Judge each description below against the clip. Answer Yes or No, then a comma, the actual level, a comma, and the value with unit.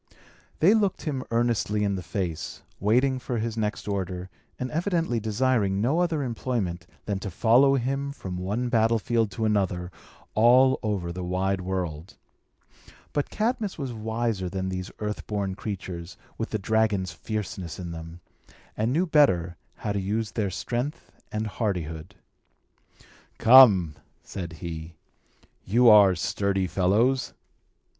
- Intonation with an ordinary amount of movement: Yes, average, 4.7 semitones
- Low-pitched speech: Yes, low, 105 Hz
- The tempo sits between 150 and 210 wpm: No, slow, 135 wpm